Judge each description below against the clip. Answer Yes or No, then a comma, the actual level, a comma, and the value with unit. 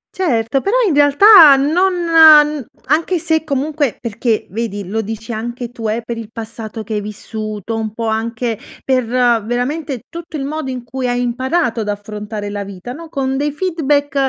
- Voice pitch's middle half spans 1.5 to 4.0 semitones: No, average, 5.1 semitones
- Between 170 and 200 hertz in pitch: No, high, 245 Hz